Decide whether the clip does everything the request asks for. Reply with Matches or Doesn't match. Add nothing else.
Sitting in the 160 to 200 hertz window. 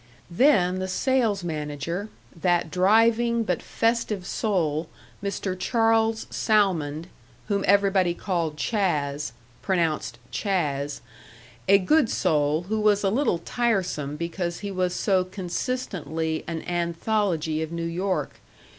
Matches